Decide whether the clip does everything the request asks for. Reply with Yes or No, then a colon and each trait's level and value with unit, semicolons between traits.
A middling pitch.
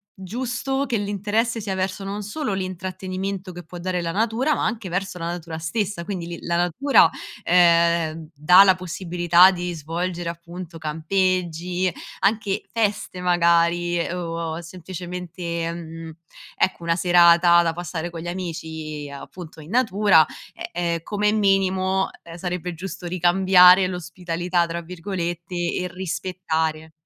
Yes: medium, 180 Hz